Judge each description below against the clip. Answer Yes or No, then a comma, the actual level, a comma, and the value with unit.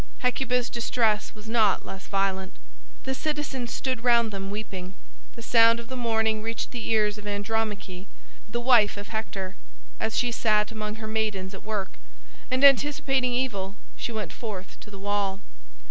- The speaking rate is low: No, average, 160 wpm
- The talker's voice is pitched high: Yes, high, 220 Hz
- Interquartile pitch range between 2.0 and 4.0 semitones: Yes, average, 2.8 semitones